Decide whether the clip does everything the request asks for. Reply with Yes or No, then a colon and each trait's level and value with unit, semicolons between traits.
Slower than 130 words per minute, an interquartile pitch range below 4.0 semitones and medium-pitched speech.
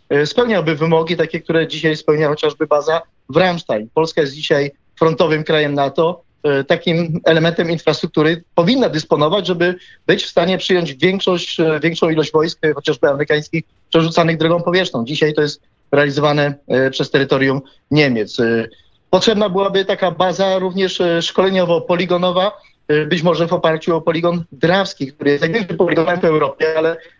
No: average, 140 wpm; average, 2.7 semitones; medium, 165 Hz